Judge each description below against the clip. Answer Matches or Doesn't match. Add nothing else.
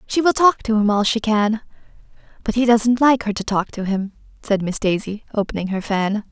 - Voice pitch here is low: Doesn't match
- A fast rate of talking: Matches